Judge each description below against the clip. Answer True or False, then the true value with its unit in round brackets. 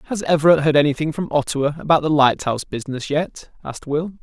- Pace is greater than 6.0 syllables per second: True (6.5 syllables/s)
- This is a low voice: False (150 Hz)